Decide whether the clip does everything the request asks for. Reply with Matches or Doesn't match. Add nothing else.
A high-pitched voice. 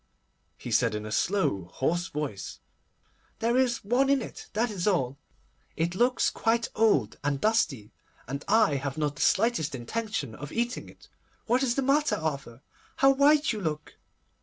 Matches